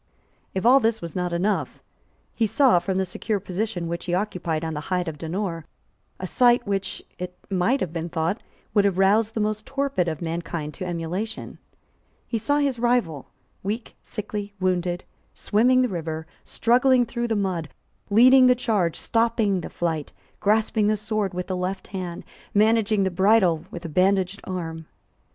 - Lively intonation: No, average, 4.3 semitones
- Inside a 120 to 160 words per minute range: No, average, 170 wpm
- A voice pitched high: Yes, high, 195 Hz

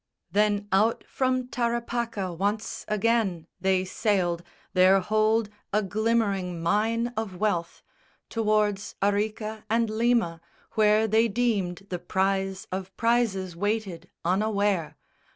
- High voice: Yes, high, 210 Hz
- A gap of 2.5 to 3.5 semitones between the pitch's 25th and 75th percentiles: Yes, average, 2.9 semitones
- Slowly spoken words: Yes, slow, 110 wpm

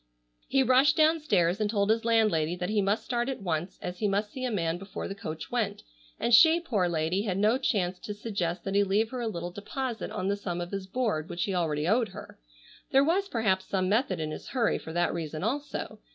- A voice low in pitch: No, high, 200 Hz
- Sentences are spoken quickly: Yes, fast, 230 wpm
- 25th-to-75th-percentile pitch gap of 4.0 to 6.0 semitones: Yes, average, 5.0 semitones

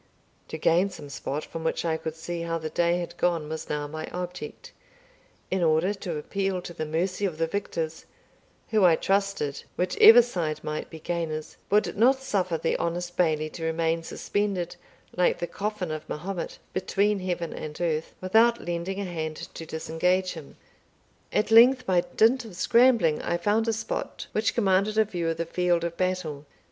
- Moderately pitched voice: Yes, medium, 175 Hz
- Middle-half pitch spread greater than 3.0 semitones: Yes, average, 3.5 semitones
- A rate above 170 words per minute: Yes, average, 180 wpm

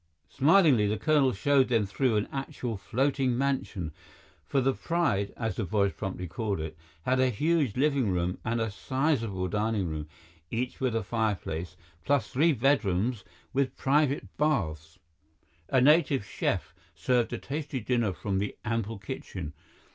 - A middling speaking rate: Yes, average, 150 wpm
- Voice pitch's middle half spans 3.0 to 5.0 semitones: No, wide, 5.5 semitones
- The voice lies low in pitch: Yes, low, 115 Hz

